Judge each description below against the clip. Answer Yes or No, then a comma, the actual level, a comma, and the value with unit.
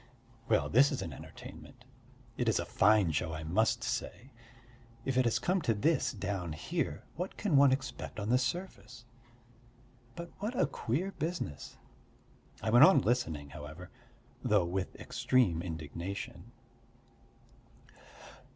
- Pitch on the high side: No, low, 115 Hz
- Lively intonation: Yes, wide, 7.9 semitones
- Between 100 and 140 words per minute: Yes, slow, 135 wpm